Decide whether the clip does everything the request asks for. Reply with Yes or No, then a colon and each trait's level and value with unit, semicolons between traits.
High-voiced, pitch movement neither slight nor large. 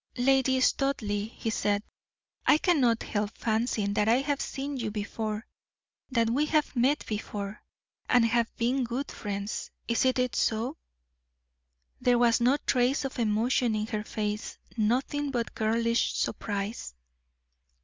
Yes: high, 235 Hz; average, 3.4 semitones